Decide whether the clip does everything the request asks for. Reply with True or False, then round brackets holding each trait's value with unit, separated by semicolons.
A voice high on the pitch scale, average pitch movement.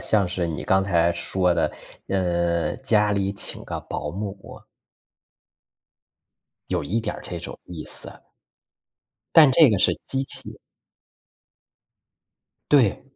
False (95 Hz; 3.7 semitones)